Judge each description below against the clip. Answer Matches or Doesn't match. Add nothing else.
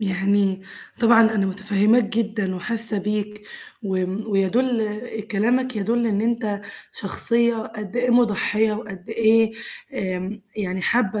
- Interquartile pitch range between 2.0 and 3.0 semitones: Matches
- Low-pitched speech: Doesn't match